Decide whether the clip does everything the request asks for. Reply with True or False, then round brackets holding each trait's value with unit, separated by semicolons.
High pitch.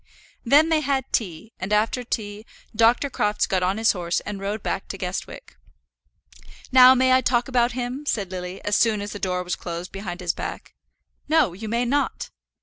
True (215 Hz)